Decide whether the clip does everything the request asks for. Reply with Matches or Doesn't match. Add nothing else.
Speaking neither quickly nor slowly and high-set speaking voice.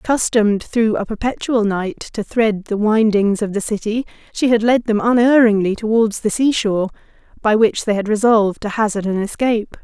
Matches